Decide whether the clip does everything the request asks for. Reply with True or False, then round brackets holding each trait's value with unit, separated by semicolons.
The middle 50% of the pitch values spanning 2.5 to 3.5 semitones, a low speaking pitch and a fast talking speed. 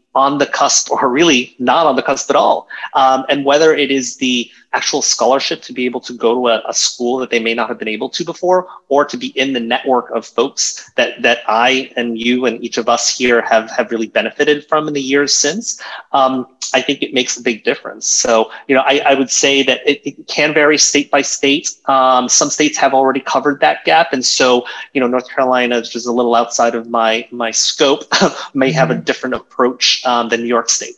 True (3.0 semitones; 130 Hz; 235 wpm)